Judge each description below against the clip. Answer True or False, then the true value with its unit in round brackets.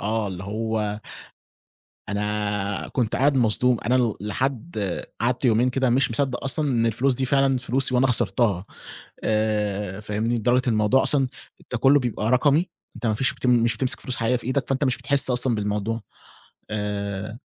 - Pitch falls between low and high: False (120 Hz)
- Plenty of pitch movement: False (3.5 semitones)